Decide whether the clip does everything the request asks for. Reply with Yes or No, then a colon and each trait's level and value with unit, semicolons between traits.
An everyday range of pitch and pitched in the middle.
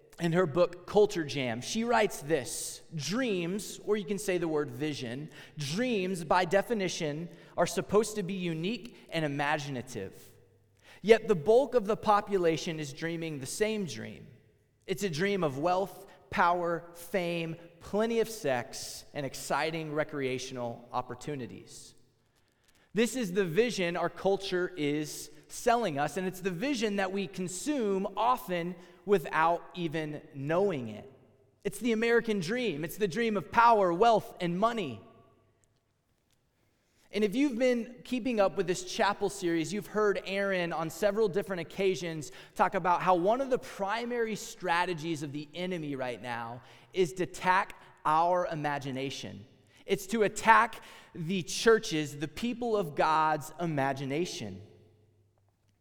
No: wide, 6.2 semitones; medium, 175 Hz